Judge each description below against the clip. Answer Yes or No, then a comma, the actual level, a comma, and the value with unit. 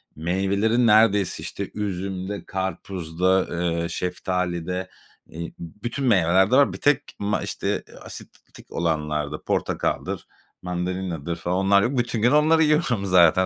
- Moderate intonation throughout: Yes, average, 3.6 semitones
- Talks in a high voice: No, very low, 95 Hz